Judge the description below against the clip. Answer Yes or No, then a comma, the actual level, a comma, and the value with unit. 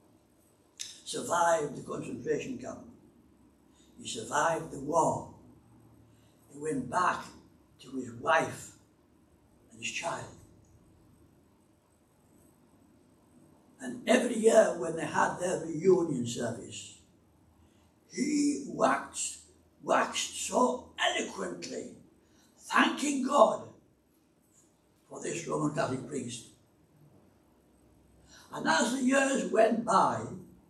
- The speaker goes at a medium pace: No, slow, 85 wpm